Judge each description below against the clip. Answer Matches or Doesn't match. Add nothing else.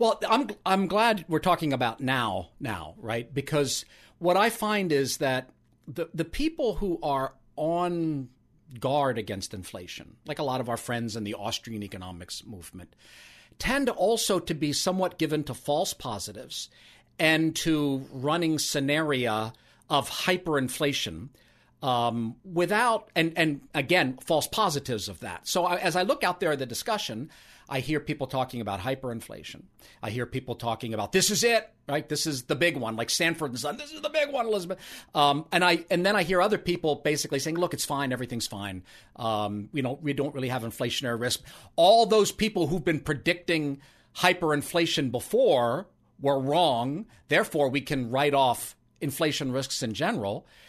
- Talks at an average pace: Matches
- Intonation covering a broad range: Matches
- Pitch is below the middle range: Doesn't match